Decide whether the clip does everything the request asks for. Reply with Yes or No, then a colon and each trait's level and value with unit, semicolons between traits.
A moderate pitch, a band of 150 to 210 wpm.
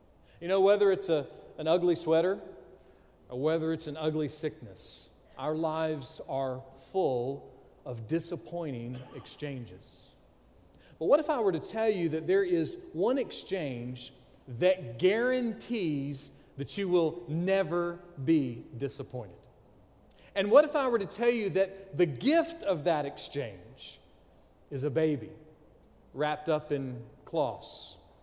No: medium, 155 Hz; slow, 135 wpm